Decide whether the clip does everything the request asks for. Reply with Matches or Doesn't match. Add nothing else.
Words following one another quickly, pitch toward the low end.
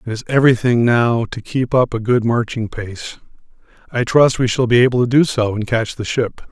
Matches